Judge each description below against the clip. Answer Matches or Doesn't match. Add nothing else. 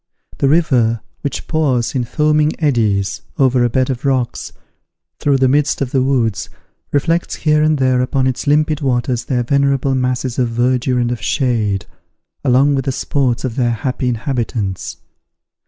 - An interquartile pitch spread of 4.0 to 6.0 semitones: Doesn't match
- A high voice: Doesn't match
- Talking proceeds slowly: Doesn't match